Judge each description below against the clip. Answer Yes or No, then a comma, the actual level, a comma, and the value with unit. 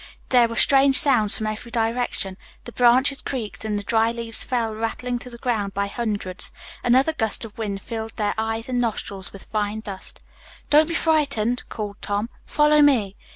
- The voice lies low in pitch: No, high, 230 Hz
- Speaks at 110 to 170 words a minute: No, average, 180 wpm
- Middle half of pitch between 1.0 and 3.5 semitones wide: Yes, average, 2.9 semitones